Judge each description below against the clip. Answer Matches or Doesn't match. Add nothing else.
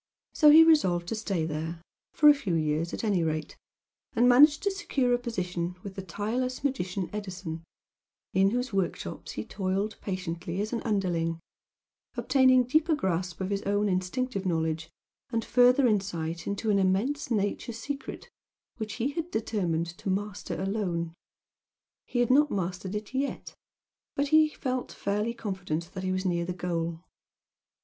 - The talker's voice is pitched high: Matches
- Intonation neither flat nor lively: Doesn't match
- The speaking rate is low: Doesn't match